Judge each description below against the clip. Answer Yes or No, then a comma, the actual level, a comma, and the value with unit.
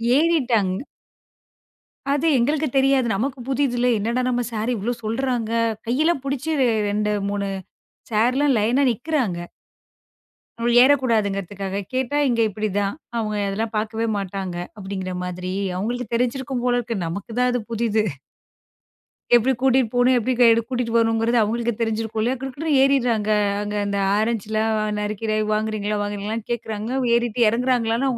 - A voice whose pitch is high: Yes, high, 230 Hz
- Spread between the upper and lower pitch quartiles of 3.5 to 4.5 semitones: No, average, 3.0 semitones